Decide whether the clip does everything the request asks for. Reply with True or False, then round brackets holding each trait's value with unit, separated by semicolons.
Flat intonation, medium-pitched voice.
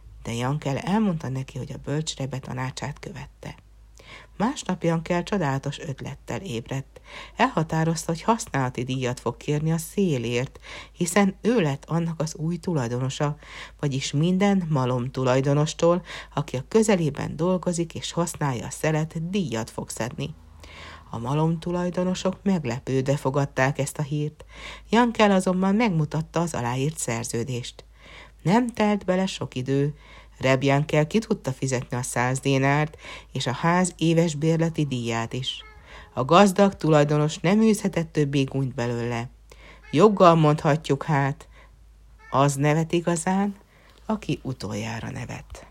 False (4.9 semitones; 150 Hz)